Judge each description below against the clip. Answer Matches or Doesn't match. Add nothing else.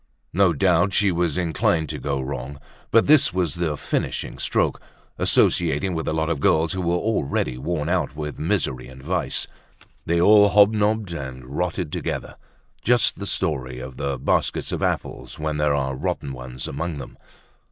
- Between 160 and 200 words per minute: Matches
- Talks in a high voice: Doesn't match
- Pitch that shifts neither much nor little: Matches